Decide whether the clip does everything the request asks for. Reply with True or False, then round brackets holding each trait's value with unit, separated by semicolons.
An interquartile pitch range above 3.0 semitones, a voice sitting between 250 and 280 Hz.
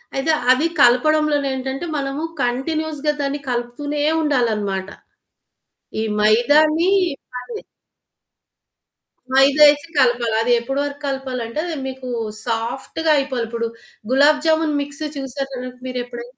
True (3.5 semitones; 270 Hz)